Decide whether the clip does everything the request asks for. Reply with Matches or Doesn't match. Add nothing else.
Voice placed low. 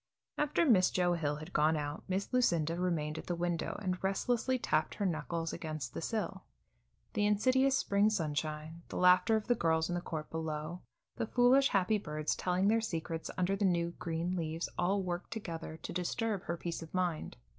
Doesn't match